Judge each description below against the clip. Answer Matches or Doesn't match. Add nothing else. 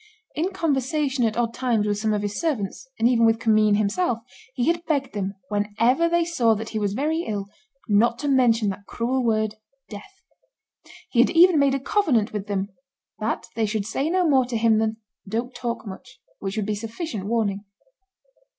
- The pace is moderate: Matches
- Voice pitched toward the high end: Matches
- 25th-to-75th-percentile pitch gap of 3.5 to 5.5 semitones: Matches